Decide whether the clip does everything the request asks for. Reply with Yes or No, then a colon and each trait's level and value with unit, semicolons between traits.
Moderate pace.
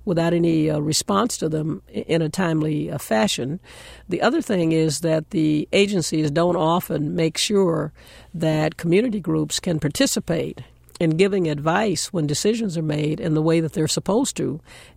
Yes: average, 165 wpm